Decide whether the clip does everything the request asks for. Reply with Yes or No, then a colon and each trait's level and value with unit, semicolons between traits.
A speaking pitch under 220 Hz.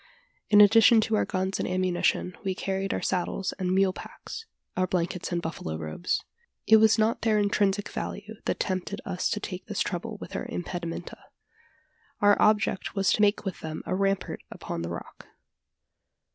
Yes: high, 190 Hz